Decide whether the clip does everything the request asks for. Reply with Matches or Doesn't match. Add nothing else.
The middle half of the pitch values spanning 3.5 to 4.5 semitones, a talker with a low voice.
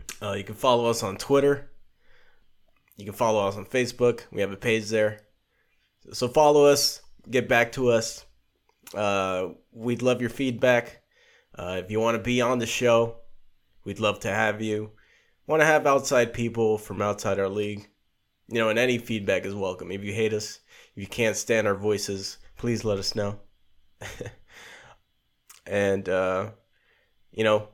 Doesn't match